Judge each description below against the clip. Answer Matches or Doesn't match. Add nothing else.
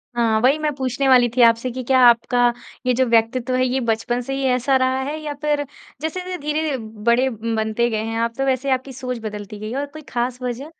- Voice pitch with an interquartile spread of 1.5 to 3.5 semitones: Matches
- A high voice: Matches